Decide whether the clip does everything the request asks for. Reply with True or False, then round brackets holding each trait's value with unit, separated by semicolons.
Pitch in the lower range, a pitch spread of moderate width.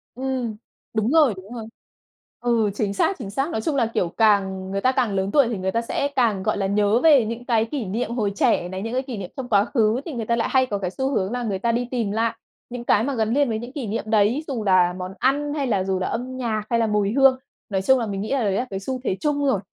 False (230 Hz; 4.2 semitones)